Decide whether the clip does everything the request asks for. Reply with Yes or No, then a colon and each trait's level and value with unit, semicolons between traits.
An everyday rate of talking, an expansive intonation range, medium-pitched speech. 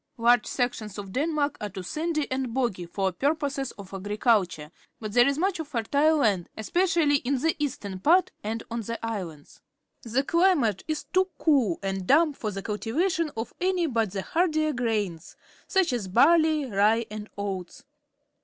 No: average, 165 wpm; wide, 7.0 semitones; high, 245 Hz